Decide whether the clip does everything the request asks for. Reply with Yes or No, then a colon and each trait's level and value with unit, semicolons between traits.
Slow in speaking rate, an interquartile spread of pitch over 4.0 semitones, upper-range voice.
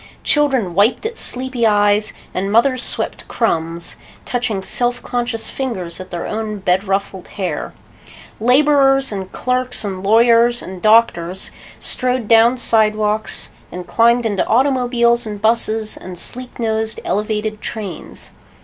No: slow, 130 wpm; average, 3.4 semitones; high, 220 Hz